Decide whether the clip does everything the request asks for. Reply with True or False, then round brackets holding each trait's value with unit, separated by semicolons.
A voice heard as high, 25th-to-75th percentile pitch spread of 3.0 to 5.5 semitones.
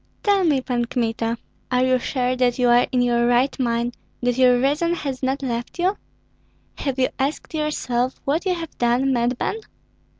False (255 Hz; 2.6 semitones)